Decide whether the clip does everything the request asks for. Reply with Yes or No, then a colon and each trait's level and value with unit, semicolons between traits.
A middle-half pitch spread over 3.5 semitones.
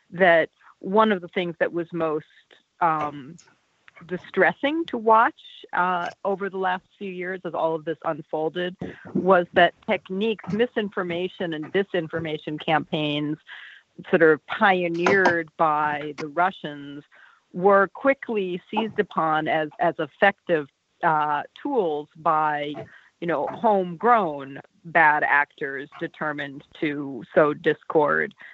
Yes: average, 4.1 semitones